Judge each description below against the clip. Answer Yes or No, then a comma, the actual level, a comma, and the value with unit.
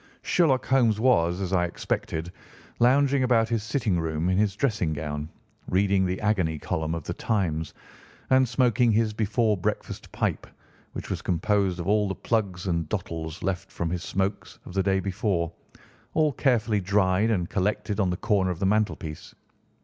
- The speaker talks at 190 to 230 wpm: No, average, 170 wpm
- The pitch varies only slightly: No, average, 4.0 semitones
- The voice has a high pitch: No, low, 100 Hz